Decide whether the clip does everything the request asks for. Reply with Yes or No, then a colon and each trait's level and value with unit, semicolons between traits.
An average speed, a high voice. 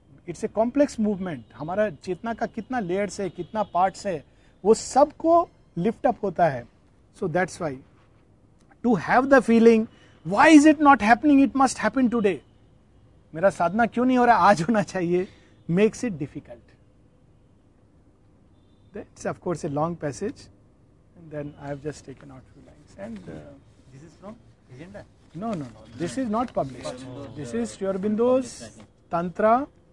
No: average, 135 wpm; medium, 180 Hz